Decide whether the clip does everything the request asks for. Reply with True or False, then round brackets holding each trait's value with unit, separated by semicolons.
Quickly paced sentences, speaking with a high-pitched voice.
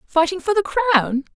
False (175 wpm; 340 Hz)